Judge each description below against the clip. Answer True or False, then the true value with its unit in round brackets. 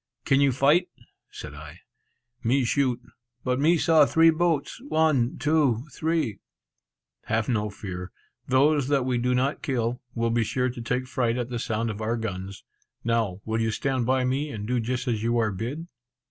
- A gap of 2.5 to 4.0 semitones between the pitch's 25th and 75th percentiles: True (3.7 semitones)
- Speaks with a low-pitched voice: True (125 Hz)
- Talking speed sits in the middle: True (180 wpm)